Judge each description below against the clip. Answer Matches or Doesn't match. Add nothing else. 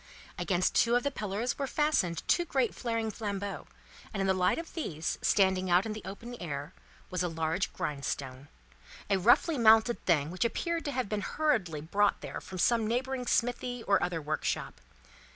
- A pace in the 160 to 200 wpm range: Matches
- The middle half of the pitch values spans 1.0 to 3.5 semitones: Doesn't match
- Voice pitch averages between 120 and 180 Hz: Doesn't match